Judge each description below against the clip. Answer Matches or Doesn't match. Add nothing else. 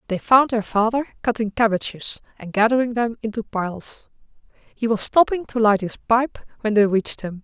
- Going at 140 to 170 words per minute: Doesn't match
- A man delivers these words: Doesn't match